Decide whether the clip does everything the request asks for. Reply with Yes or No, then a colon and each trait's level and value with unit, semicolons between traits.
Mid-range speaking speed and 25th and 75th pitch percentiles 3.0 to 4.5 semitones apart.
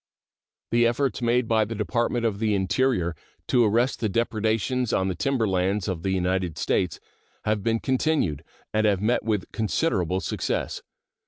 Yes: average, 160 wpm; average, 3.8 semitones